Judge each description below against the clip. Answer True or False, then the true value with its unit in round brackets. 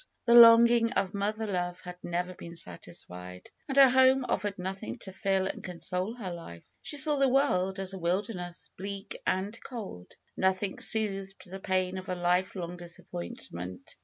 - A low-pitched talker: False (190 Hz)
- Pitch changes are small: False (3.6 semitones)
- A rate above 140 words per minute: True (160 wpm)